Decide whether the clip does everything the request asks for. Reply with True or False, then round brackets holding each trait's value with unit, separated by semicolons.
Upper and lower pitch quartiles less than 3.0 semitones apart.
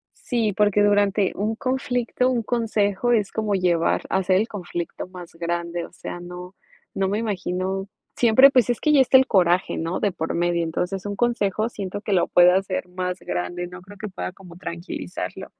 False (3.4 semitones)